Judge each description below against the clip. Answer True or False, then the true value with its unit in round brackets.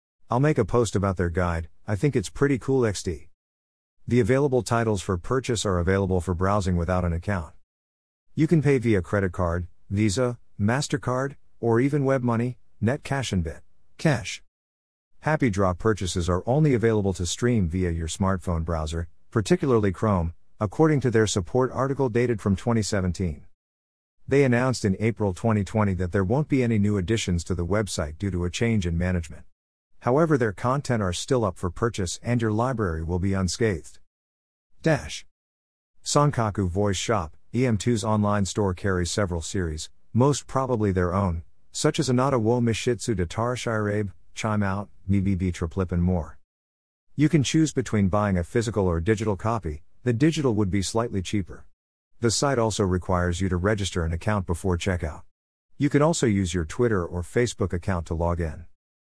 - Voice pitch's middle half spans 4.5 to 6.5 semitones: True (5.2 semitones)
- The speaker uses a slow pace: False (165 wpm)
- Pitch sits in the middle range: False (100 Hz)